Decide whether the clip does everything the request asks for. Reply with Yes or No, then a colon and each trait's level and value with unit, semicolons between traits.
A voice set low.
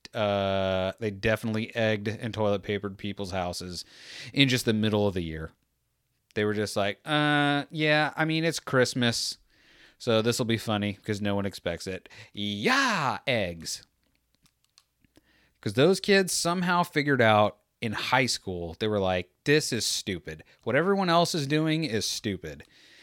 Yes: low, 110 Hz